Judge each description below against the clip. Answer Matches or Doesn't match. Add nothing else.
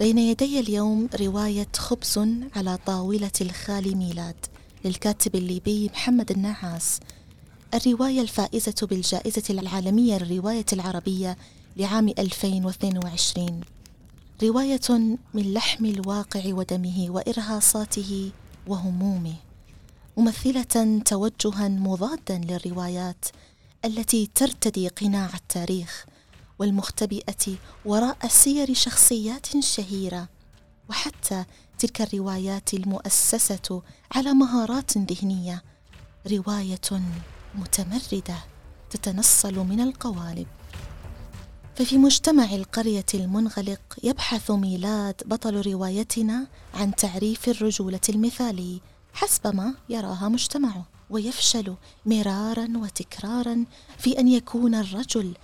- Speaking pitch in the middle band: Doesn't match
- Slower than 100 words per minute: Matches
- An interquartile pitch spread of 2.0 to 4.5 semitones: Matches